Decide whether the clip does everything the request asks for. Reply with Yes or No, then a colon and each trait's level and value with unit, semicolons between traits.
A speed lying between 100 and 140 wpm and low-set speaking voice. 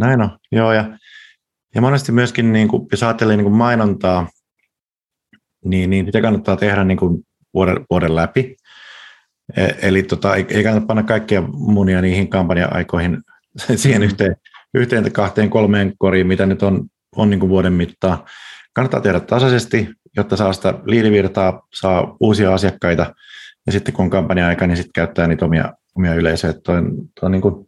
No: fast, 155 wpm; low, 100 Hz